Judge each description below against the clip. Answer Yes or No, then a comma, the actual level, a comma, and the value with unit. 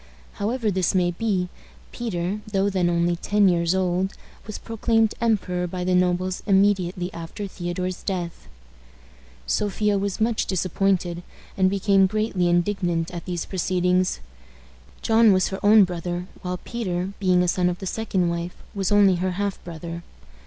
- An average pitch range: No, narrow, 2.3 semitones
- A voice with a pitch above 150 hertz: Yes, medium, 185 Hz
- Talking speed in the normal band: Yes, average, 150 wpm